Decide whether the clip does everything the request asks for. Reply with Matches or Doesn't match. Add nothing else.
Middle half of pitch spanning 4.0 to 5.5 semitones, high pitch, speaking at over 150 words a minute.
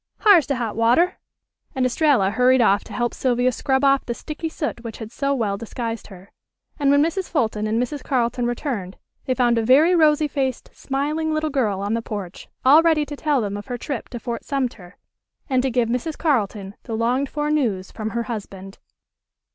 Matches